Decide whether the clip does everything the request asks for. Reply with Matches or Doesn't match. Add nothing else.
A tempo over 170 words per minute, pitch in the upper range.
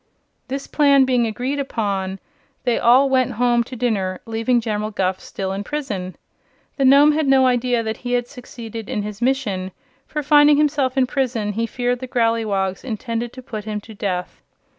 Matches